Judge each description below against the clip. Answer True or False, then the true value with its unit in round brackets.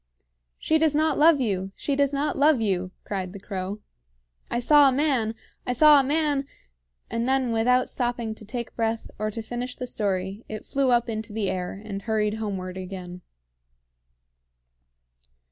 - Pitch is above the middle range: True (225 Hz)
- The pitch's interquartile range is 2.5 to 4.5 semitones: False (5.3 semitones)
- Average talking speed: True (170 wpm)